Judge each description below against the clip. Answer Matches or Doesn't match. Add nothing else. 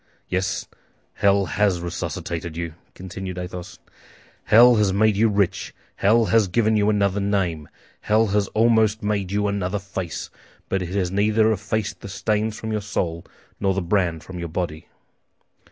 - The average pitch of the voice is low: Matches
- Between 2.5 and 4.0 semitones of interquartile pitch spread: Matches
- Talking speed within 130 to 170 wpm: Matches